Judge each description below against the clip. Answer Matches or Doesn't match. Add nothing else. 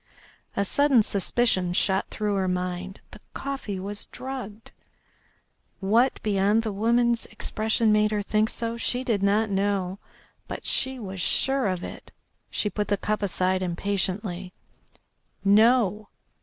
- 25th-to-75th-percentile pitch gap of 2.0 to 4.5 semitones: Matches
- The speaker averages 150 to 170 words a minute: Doesn't match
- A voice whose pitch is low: Doesn't match